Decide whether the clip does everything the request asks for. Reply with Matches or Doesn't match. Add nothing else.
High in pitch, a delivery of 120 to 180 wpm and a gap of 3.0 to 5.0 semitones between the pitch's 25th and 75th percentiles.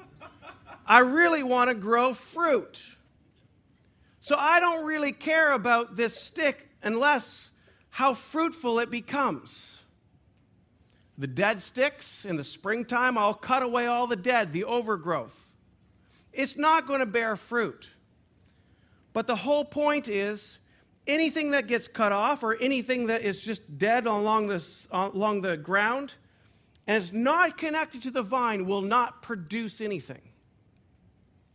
Doesn't match